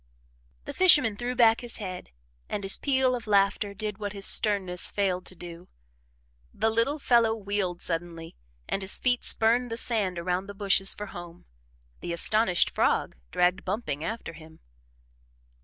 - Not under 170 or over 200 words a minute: No, average, 155 wpm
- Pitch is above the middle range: Yes, high, 200 Hz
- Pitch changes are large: No, average, 4.0 semitones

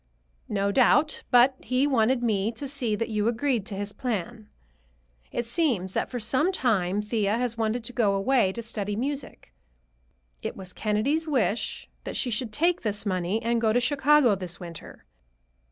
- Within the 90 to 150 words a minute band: No, average, 170 wpm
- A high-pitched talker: Yes, high, 230 Hz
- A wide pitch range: No, average, 3.8 semitones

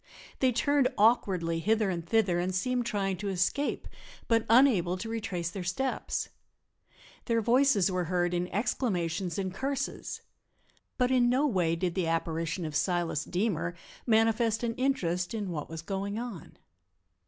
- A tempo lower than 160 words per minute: Yes, average, 150 wpm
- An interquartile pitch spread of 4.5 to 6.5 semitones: Yes, average, 4.9 semitones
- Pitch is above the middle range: Yes, high, 195 Hz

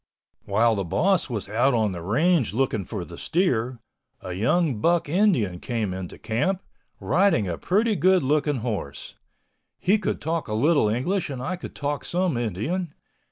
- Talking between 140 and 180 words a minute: Yes, average, 165 wpm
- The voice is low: Yes, low, 130 Hz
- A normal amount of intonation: No, wide, 8.5 semitones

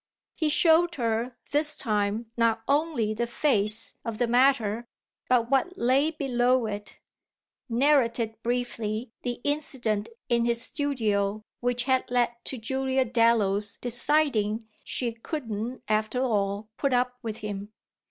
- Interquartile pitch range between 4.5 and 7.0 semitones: No, average, 3.3 semitones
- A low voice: No, high, 240 Hz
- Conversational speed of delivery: No, slow, 130 wpm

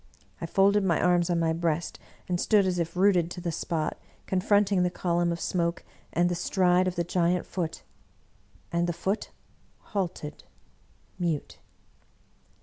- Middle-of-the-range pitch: Yes, medium, 175 Hz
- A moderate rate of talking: Yes, average, 150 wpm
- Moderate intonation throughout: No, narrow, 1.5 semitones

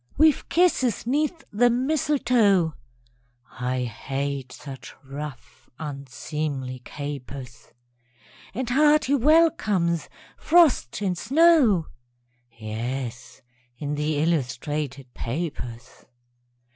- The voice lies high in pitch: No, medium, 155 Hz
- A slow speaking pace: Yes, slow, 80 wpm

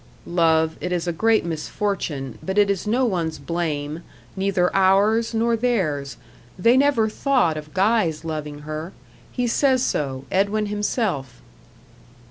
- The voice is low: No, medium, 185 Hz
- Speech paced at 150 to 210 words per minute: No, slow, 135 wpm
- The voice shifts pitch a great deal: Yes, wide, 5.9 semitones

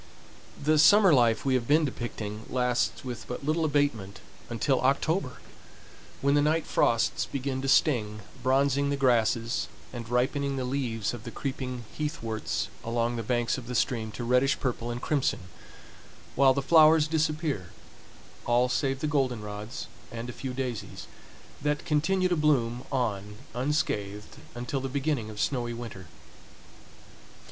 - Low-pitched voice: Yes, low, 130 Hz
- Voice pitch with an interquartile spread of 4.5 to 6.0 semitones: No, average, 3.4 semitones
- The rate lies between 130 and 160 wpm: Yes, average, 145 wpm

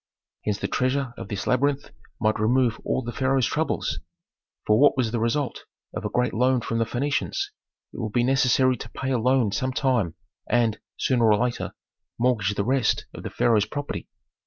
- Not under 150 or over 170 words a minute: No, average, 185 wpm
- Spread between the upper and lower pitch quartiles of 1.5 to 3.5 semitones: Yes, average, 2.9 semitones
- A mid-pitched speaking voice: No, low, 125 Hz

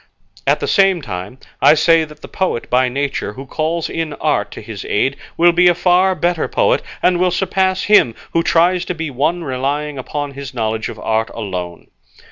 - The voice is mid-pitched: Yes, medium, 150 Hz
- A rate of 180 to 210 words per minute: Yes, average, 195 wpm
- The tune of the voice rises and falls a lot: Yes, wide, 5.9 semitones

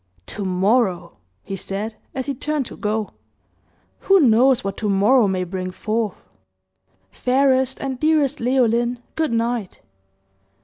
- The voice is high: Yes, high, 235 Hz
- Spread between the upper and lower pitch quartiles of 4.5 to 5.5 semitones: Yes, average, 4.8 semitones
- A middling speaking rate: No, slow, 130 wpm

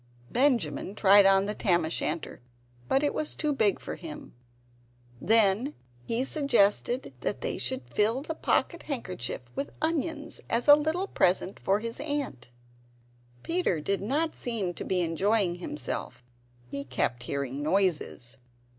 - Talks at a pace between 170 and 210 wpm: No, average, 145 wpm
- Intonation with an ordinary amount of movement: No, wide, 9.0 semitones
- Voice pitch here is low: No, high, 205 Hz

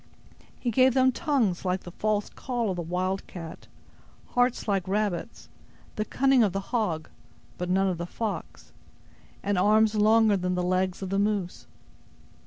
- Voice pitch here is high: Yes, high, 200 Hz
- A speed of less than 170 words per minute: Yes, average, 160 wpm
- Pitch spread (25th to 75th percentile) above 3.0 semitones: Yes, average, 3.4 semitones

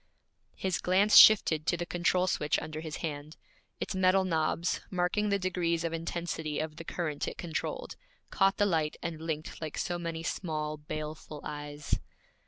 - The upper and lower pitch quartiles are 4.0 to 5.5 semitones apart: No, average, 2.9 semitones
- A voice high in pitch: No, medium, 165 Hz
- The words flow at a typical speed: Yes, average, 165 wpm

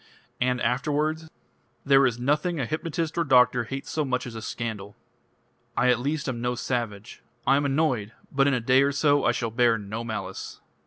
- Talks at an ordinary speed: Yes, average, 195 wpm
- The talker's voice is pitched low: Yes, low, 125 Hz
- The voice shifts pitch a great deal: No, average, 3.5 semitones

